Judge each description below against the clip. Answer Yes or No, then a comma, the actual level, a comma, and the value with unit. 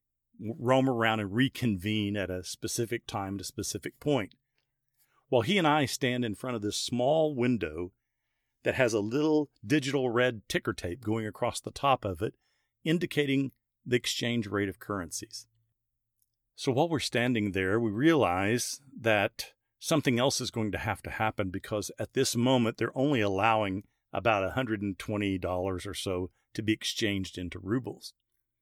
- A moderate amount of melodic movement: Yes, average, 3.7 semitones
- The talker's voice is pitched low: Yes, low, 115 Hz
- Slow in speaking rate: No, average, 155 wpm